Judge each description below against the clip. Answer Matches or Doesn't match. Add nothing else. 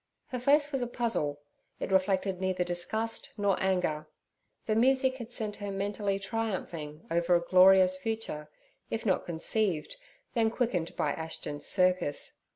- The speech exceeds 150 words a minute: Doesn't match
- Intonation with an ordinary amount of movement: Matches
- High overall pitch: Matches